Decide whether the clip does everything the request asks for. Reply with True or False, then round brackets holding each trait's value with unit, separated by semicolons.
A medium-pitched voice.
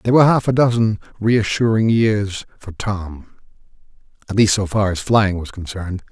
False (105 Hz)